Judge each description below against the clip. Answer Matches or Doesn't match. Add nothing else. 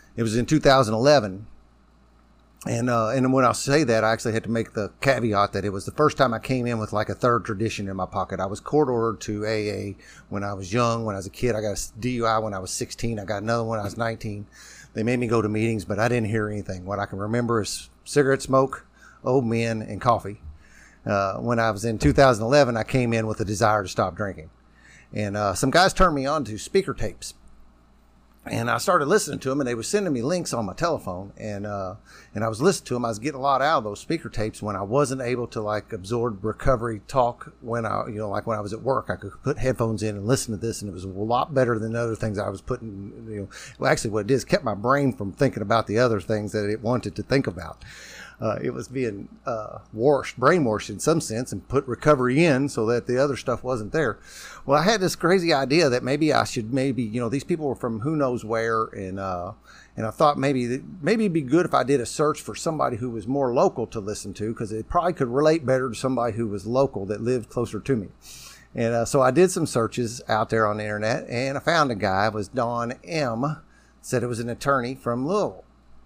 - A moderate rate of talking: Doesn't match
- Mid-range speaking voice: Doesn't match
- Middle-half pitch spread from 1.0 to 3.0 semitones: Doesn't match